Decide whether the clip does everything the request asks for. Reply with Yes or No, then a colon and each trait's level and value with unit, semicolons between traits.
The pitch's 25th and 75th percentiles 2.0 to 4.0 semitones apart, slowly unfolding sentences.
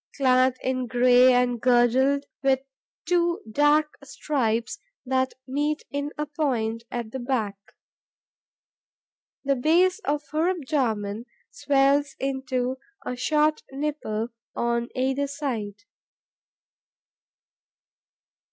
Yes: average, 3.2 semitones; slow, 95 wpm